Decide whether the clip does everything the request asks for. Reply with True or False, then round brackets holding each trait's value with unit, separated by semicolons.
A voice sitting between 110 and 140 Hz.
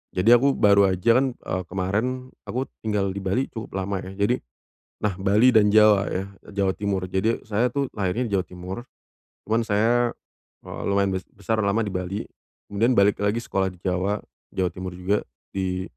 False (100 Hz)